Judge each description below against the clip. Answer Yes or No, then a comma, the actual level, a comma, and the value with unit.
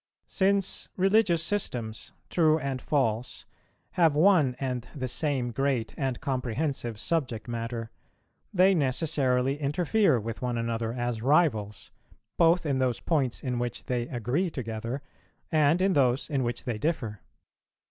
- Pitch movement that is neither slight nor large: Yes, average, 5.0 semitones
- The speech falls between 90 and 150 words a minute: Yes, slow, 135 wpm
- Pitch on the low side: Yes, low, 130 Hz